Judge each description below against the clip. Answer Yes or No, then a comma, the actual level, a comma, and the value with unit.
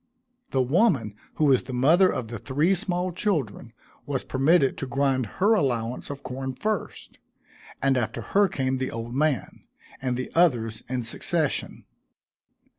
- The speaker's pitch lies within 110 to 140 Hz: Yes, low, 135 Hz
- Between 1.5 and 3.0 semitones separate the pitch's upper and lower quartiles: No, average, 5.1 semitones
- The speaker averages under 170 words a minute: Yes, average, 150 wpm